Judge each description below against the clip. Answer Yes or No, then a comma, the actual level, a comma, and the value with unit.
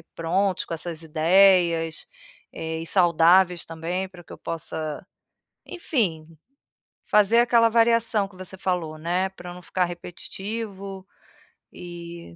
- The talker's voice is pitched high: No, medium, 180 Hz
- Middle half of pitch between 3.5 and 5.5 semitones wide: No, average, 2.8 semitones